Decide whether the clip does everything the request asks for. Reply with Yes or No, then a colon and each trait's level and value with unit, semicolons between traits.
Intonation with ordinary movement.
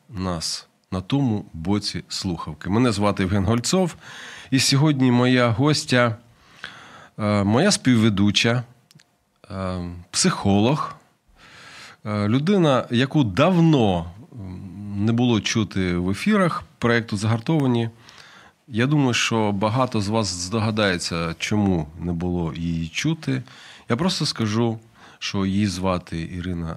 Yes: average, 5.0 semitones